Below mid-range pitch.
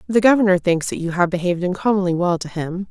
No: medium, 185 Hz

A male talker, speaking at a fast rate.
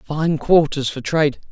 No: male; average, 160 wpm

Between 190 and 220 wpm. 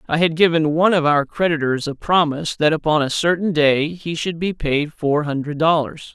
Yes: fast, 205 wpm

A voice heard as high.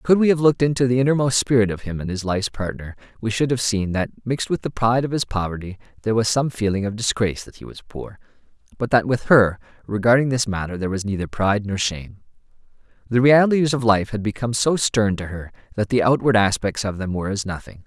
No: low, 110 Hz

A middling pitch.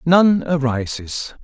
Yes: medium, 150 Hz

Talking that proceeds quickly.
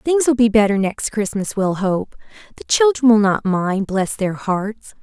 No: average, 190 wpm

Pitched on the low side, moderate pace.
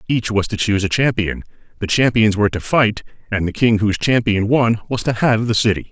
No: low, 110 Hz; fast, 225 wpm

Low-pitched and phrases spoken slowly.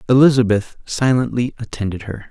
Yes: low, 115 Hz; slow, 105 wpm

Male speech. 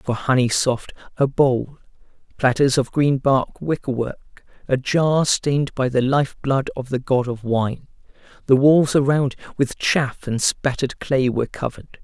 Yes: male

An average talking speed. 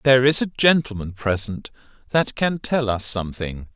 Yes: average, 160 wpm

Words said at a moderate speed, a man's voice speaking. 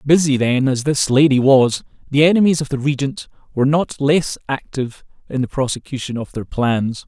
Yes: average, 180 wpm; male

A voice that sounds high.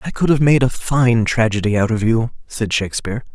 No: low, 115 Hz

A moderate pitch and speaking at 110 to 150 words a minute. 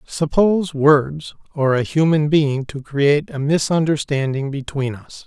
Yes: medium, 145 Hz; slow, 135 wpm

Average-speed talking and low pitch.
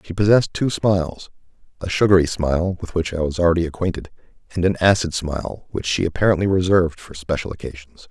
Yes: average, 170 wpm; very low, 85 Hz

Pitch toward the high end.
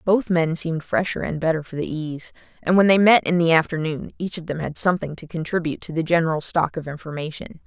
No: medium, 165 Hz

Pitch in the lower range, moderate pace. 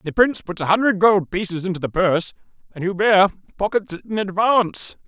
No: high, 190 Hz; average, 190 wpm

